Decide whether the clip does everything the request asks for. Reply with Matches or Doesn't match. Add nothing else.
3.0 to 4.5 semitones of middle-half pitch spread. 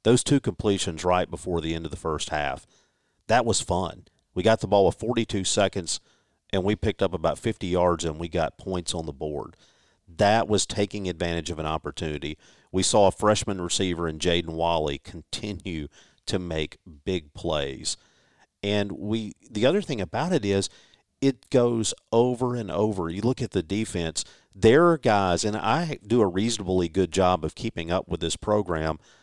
Matches